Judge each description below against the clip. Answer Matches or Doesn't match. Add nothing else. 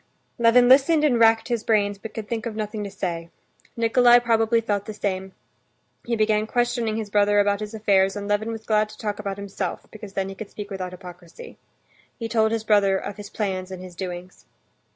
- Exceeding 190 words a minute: Matches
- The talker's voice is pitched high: Matches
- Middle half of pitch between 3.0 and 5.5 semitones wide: Doesn't match